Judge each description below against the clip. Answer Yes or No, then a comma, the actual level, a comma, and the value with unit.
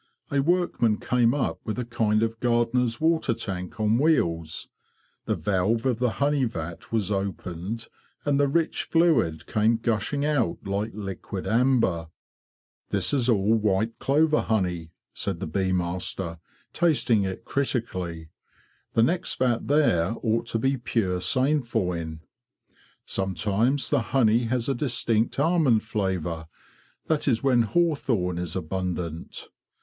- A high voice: No, low, 115 Hz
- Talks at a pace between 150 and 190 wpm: No, average, 140 wpm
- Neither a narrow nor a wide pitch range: No, wide, 5.8 semitones